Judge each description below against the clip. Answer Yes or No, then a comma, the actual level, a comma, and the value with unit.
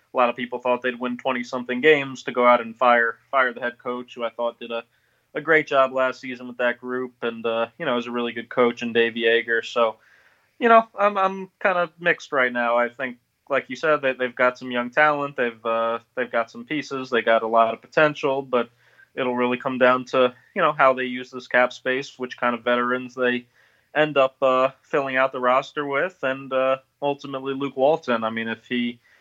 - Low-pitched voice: Yes, low, 125 Hz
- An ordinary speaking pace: No, fast, 230 wpm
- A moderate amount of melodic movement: No, narrow, 1.8 semitones